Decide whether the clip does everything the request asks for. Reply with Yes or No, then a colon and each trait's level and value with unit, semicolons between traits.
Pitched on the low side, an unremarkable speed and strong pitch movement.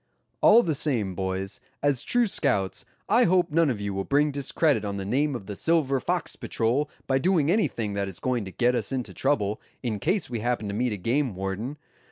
No: low, 125 Hz; fast, 215 wpm; wide, 6.6 semitones